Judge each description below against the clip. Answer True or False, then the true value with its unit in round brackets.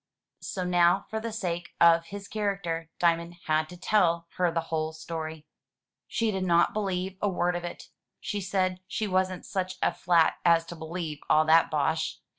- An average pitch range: False (2.3 semitones)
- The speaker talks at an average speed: True (180 wpm)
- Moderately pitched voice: True (175 Hz)